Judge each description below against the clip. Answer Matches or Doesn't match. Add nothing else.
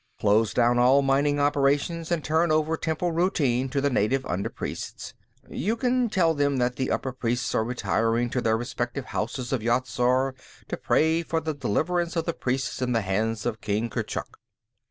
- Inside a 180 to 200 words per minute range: Matches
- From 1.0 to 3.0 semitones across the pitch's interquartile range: Doesn't match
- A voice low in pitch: Matches